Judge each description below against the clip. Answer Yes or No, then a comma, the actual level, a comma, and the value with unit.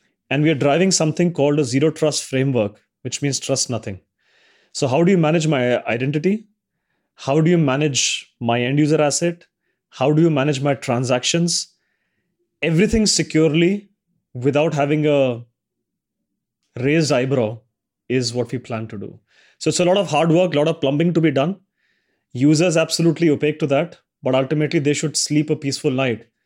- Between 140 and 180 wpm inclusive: Yes, average, 170 wpm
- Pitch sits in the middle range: Yes, medium, 150 Hz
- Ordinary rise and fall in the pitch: Yes, average, 4.0 semitones